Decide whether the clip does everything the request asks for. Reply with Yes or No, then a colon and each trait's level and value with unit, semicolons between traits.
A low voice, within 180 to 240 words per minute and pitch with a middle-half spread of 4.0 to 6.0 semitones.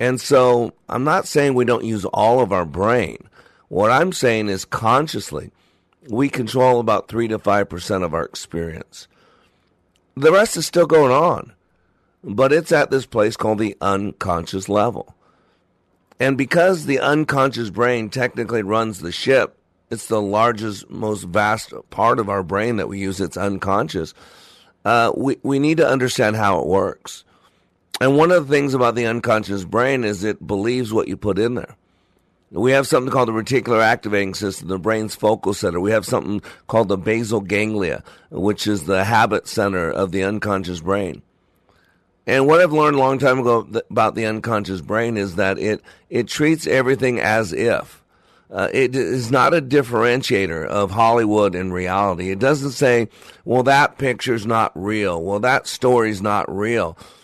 No: low, 110 Hz; average, 170 wpm; average, 4.4 semitones